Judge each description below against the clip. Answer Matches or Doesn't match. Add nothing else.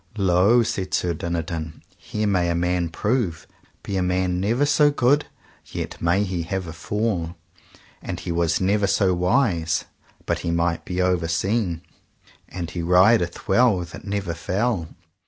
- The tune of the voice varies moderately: Matches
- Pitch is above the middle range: Doesn't match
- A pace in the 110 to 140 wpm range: Doesn't match